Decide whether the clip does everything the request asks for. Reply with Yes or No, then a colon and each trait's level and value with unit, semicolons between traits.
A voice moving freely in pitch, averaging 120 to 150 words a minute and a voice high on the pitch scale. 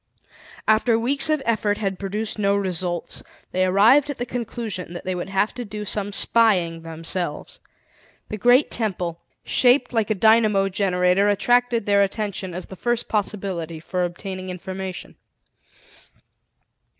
No: average, 3.6 semitones; average, 140 wpm; high, 200 Hz